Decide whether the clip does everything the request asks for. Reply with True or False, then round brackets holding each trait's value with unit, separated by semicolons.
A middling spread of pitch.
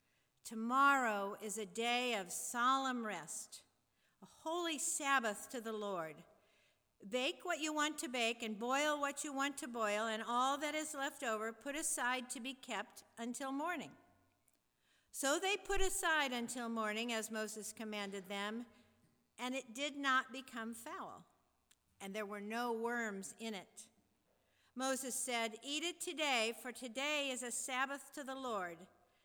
True (4.2 semitones)